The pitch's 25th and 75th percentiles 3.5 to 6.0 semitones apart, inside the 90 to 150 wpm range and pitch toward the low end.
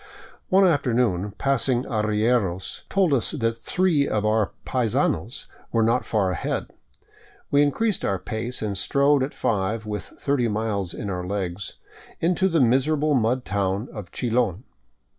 Yes: average, 5.2 semitones; average, 140 wpm; low, 115 Hz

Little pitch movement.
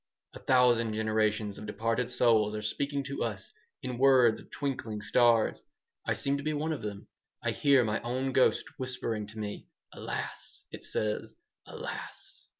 No: average, 3.5 semitones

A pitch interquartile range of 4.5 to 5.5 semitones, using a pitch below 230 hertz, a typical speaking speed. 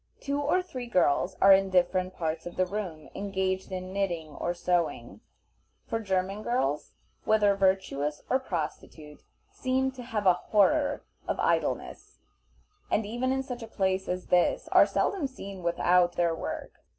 Yes: average, 5.2 semitones; high, 190 Hz; average, 155 wpm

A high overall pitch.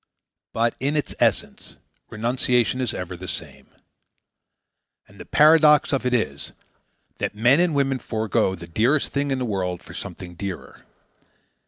No: low, 120 Hz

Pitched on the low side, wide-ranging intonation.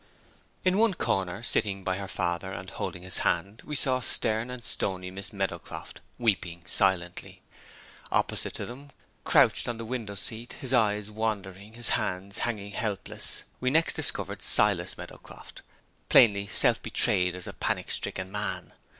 No: low, 100 Hz; average, 3.9 semitones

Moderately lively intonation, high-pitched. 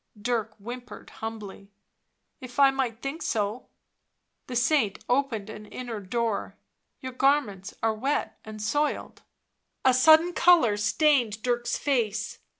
Yes: average, 4.1 semitones; high, 240 Hz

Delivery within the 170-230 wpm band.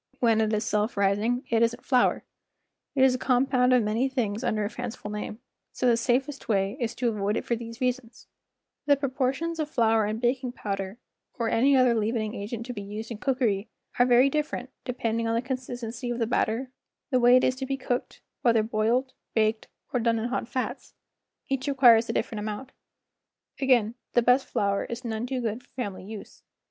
Yes: average, 200 wpm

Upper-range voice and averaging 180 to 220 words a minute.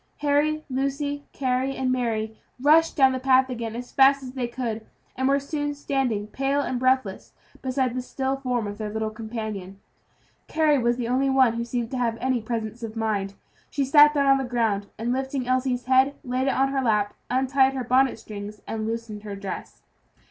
Yes: very high, 255 Hz; average, 195 wpm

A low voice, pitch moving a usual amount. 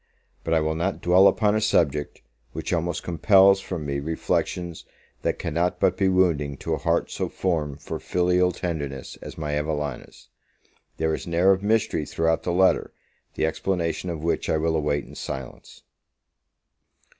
Yes: very low, 85 Hz; average, 3.3 semitones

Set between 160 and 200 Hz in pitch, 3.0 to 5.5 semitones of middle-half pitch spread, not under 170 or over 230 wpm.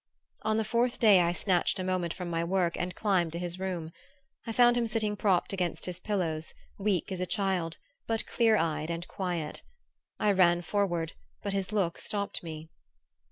Yes: medium, 185 Hz; average, 3.3 semitones; average, 185 wpm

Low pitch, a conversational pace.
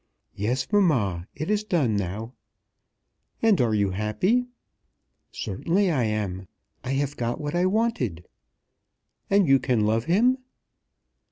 No: low, 130 Hz; slow, 125 wpm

